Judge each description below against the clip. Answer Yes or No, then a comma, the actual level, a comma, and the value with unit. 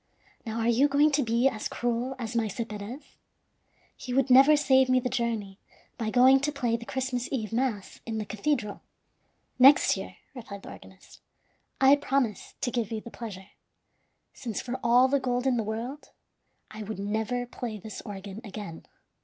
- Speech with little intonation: No, average, 3.3 semitones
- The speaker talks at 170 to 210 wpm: Yes, average, 175 wpm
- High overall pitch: Yes, high, 235 Hz